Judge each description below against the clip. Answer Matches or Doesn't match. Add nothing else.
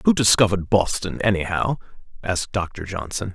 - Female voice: Doesn't match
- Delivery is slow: Matches